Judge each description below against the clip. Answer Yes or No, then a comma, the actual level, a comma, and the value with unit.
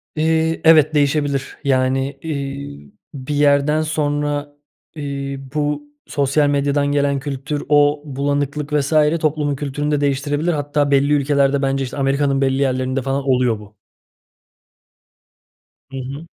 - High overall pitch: No, medium, 140 Hz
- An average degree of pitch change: No, narrow, 1.3 semitones